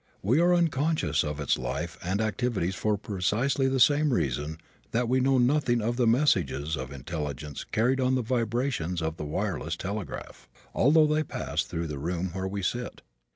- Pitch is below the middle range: Yes, low, 105 Hz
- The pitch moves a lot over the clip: Yes, wide, 7.8 semitones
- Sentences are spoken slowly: No, average, 175 wpm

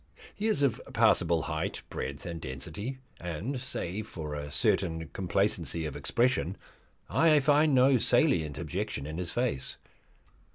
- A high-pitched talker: No, very low, 90 Hz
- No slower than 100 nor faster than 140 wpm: Yes, slow, 135 wpm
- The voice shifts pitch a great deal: Yes, wide, 8.4 semitones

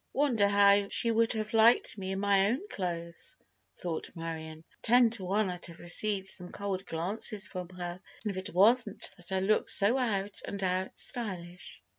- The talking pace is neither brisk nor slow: Yes, average, 175 wpm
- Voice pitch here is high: Yes, high, 195 Hz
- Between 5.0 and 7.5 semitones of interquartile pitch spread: No, average, 3.1 semitones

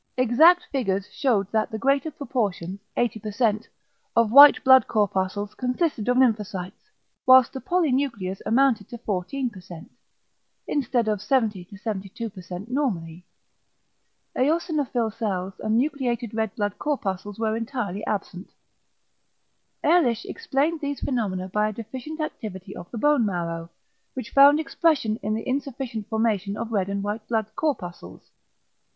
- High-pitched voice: Yes, high, 225 Hz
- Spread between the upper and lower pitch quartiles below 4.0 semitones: No, average, 4.9 semitones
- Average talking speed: No, slow, 125 wpm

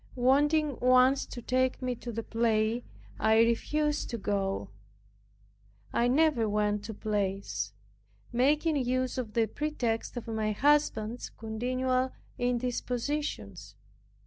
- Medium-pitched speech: No, high, 245 Hz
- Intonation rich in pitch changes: No, average, 3.0 semitones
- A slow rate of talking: Yes, slow, 115 wpm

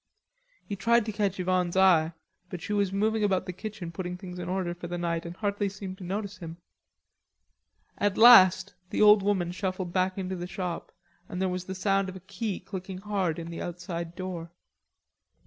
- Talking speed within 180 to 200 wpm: Yes, average, 190 wpm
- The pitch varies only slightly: Yes, narrow, 2.2 semitones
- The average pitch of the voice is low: No, medium, 185 Hz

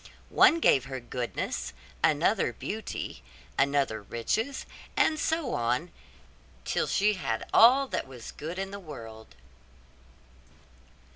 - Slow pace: Yes, slow, 115 wpm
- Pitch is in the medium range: Yes, medium, 145 Hz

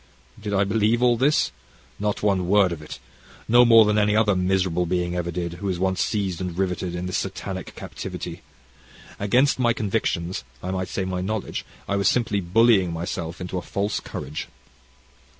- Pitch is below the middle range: Yes, very low, 95 Hz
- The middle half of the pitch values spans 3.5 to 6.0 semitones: No, average, 2.9 semitones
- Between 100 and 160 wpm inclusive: No, average, 180 wpm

